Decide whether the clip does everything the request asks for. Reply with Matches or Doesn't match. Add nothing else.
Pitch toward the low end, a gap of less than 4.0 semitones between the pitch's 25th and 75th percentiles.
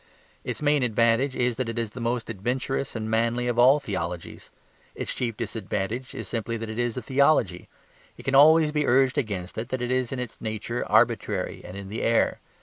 Matches